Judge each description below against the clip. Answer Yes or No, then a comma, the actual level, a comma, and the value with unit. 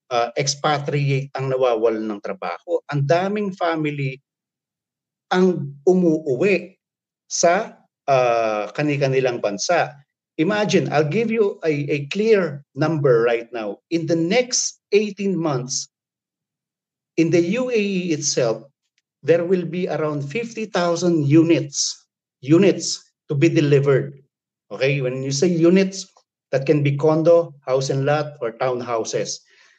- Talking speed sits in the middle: Yes, average, 120 wpm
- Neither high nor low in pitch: Yes, medium, 155 Hz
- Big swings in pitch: No, average, 4.5 semitones